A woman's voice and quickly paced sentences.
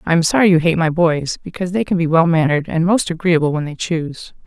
Yes: female; fast, 255 wpm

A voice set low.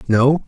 Yes: low, 130 Hz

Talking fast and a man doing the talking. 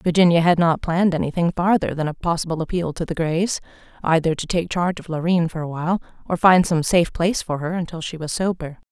No: fast, 220 wpm; female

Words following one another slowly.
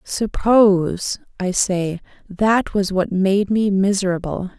Yes: slow, 120 wpm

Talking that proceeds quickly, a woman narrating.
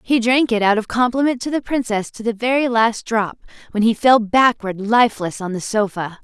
Yes: fast, 210 wpm; female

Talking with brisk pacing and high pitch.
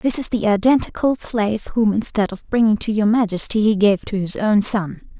Yes: fast, 210 wpm; high, 215 Hz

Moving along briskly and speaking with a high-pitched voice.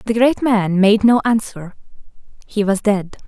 No: average, 165 wpm; high, 210 Hz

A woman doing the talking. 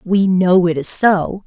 Yes: female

